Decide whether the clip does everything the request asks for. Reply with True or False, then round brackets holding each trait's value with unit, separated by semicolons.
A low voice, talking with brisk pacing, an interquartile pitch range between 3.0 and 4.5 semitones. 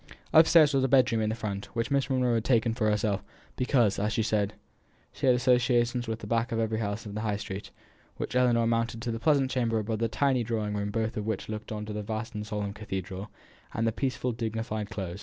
False (115 Hz; 235 wpm; 2.5 semitones)